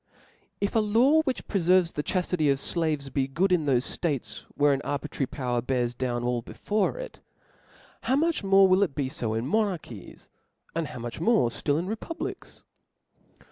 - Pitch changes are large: Yes, wide, 7.3 semitones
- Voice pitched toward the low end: No, medium, 155 Hz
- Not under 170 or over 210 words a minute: Yes, average, 175 wpm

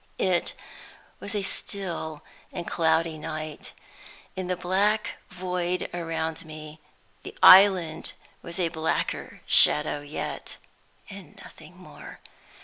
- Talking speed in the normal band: No, slow, 110 wpm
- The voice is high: No, medium, 170 Hz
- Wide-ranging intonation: No, average, 2.7 semitones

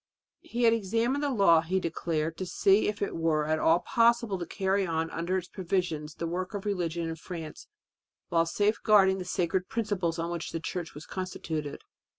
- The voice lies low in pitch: No, medium, 180 Hz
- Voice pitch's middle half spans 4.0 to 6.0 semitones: No, average, 3.4 semitones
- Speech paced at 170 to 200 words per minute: Yes, average, 185 wpm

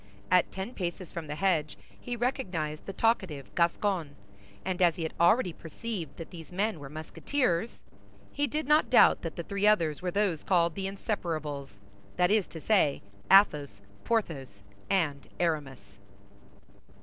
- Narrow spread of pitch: No, average, 4.8 semitones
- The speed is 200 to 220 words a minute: No, average, 150 wpm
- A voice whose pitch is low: No, medium, 175 Hz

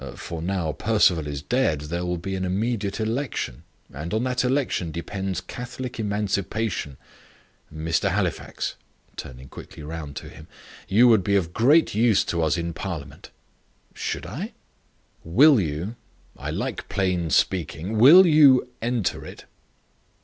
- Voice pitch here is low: Yes, very low, 95 Hz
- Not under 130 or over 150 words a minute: Yes, average, 140 wpm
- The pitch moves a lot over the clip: Yes, wide, 6.0 semitones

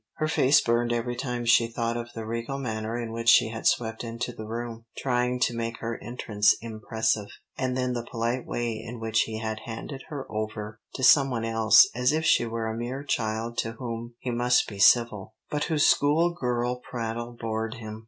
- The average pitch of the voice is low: Yes, low, 115 Hz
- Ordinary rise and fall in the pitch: No, narrow, 1.6 semitones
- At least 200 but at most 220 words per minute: Yes, fast, 205 wpm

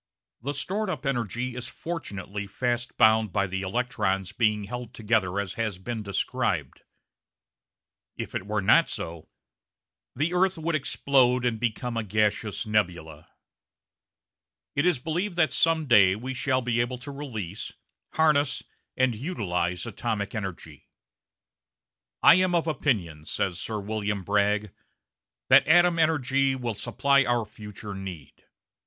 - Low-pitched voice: Yes, low, 115 Hz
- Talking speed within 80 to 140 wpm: Yes, slow, 135 wpm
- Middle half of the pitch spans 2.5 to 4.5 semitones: No, wide, 5.4 semitones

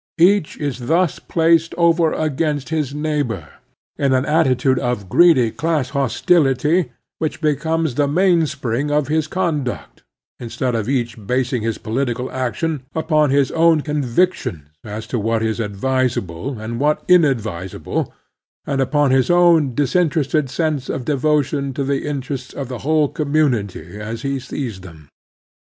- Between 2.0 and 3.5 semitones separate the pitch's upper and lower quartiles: No, average, 4.2 semitones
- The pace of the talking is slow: No, average, 150 wpm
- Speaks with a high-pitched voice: No, medium, 140 Hz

